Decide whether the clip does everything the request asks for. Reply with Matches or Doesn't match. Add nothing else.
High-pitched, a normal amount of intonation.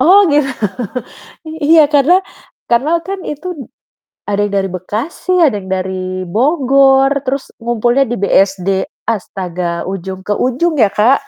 Doesn't match